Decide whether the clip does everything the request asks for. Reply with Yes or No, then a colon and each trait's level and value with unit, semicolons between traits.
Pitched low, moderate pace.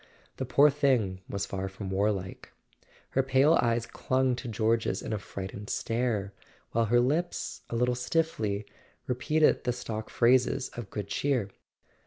Yes: low, 120 Hz; average, 150 wpm